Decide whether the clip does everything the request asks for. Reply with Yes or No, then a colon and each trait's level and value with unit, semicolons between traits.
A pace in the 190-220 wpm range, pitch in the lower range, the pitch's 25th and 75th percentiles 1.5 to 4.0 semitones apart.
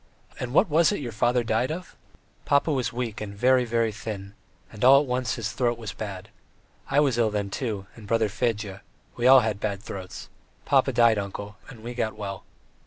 Yes: average, 200 wpm; low, 115 Hz; average, 3.4 semitones